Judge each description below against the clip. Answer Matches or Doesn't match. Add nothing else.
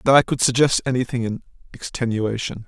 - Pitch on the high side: Doesn't match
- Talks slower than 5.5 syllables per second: Doesn't match